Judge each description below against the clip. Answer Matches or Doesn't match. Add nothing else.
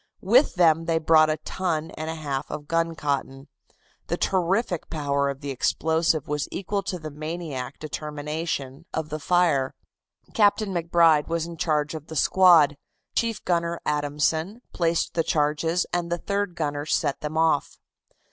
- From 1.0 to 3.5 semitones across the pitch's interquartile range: Matches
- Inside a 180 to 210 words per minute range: Doesn't match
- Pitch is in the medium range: Matches